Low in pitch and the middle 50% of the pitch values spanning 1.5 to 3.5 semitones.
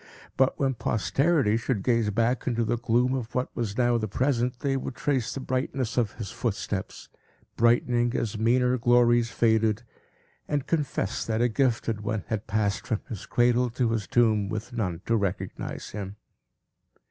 Yes: low, 115 Hz; narrow, 2.5 semitones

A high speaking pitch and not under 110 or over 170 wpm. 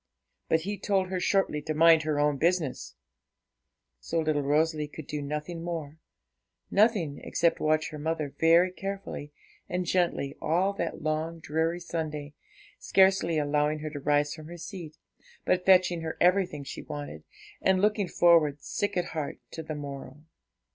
No: medium, 160 Hz; average, 155 wpm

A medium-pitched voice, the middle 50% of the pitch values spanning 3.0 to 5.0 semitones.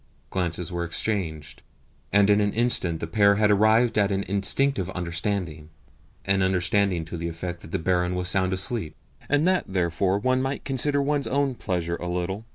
No: very low, 95 Hz; average, 3.8 semitones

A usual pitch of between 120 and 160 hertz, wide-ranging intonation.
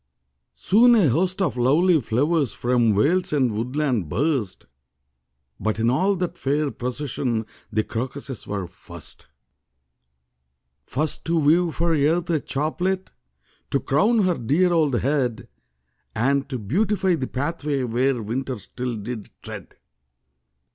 Yes: medium, 140 Hz; wide, 5.7 semitones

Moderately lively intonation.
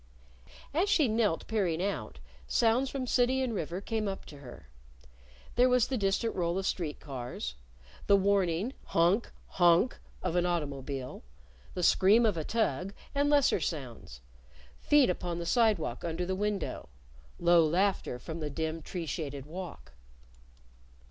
No: wide, 5.7 semitones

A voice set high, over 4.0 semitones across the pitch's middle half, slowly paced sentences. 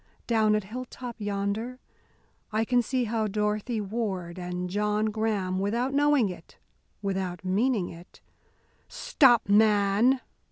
No: high, 210 Hz; average, 3.3 semitones; slow, 125 wpm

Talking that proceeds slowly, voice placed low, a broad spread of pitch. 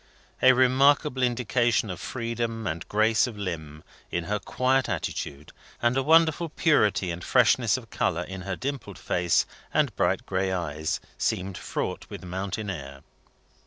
No: average, 150 wpm; low, 105 Hz; wide, 6.3 semitones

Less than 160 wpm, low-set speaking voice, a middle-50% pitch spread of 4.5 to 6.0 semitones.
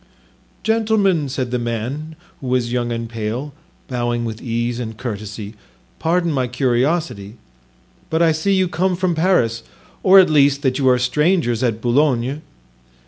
Yes: average, 150 wpm; low, 130 Hz; wide, 5.4 semitones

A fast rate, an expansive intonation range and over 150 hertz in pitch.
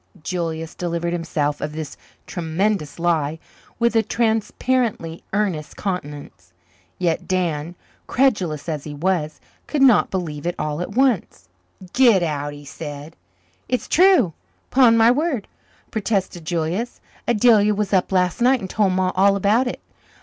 No: average, 140 wpm; wide, 5.8 semitones; medium, 185 Hz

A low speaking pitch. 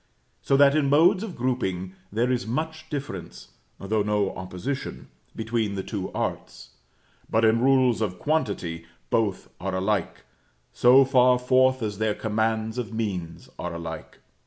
Yes: low, 110 Hz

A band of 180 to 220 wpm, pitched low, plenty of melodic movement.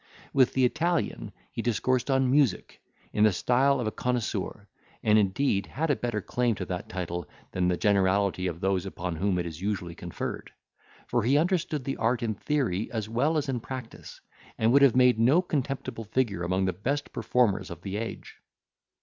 Yes: average, 185 wpm; low, 115 Hz; wide, 5.7 semitones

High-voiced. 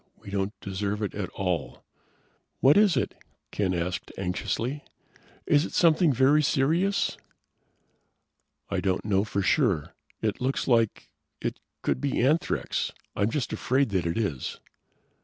No: low, 110 Hz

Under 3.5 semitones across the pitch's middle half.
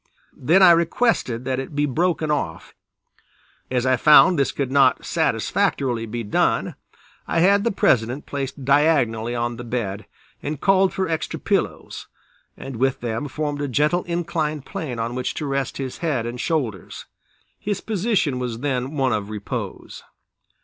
No: average, 4.8 semitones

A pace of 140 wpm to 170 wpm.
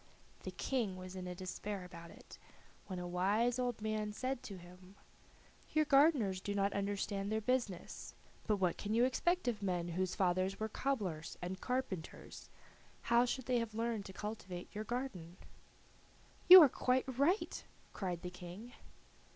Yes: average, 160 wpm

